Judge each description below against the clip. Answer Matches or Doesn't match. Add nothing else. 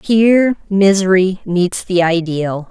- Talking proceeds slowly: Matches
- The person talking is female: Matches